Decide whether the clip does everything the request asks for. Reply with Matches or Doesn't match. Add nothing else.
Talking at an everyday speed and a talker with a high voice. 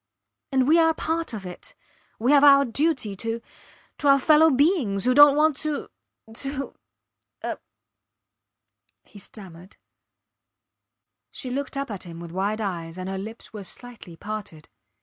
Matches